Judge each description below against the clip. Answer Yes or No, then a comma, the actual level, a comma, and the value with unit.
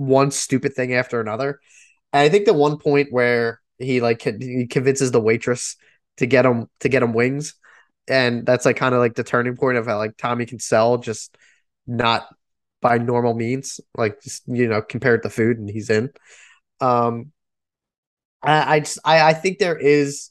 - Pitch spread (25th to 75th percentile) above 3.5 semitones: No, average, 2.8 semitones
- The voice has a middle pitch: No, low, 125 Hz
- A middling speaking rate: Yes, average, 185 wpm